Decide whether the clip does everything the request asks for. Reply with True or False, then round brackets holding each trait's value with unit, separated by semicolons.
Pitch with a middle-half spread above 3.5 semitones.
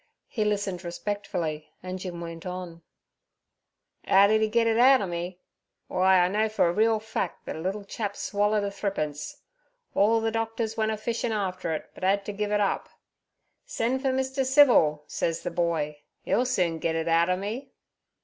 True (4.2 semitones)